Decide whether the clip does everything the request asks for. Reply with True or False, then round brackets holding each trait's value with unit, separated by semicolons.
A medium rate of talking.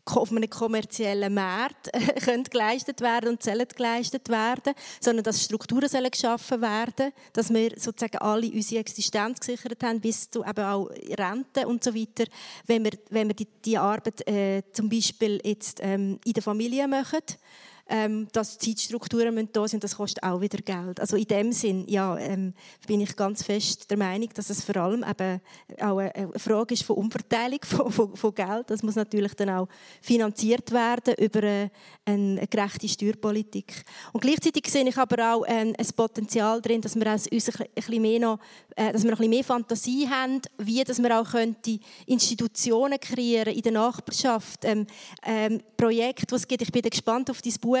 True (175 wpm)